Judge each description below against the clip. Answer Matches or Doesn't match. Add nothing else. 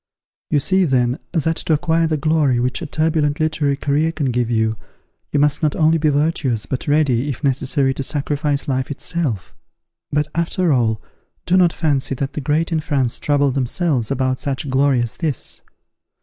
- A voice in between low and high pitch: Matches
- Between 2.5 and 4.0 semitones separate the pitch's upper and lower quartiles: Matches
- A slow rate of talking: Doesn't match